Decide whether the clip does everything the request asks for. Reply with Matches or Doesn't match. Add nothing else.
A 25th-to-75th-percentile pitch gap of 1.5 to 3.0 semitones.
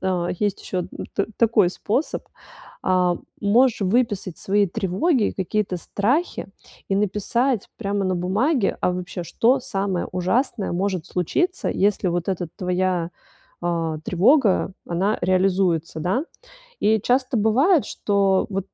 Doesn't match